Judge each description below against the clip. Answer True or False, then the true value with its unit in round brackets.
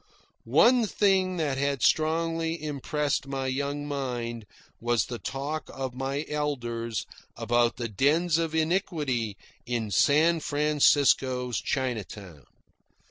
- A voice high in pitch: False (140 Hz)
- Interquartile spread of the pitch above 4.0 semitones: True (4.5 semitones)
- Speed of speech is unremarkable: False (110 wpm)